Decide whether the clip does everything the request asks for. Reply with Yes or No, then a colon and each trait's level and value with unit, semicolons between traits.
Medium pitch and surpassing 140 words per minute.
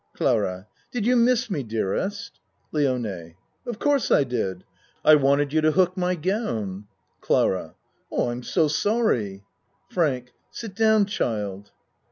No: medium, 145 Hz; slow, 135 wpm